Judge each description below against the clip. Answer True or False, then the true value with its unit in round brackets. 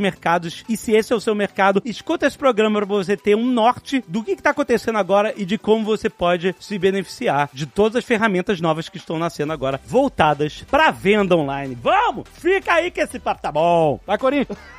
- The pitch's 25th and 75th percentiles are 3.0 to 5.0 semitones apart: False (5.4 semitones)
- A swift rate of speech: True (210 wpm)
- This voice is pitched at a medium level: False (205 Hz)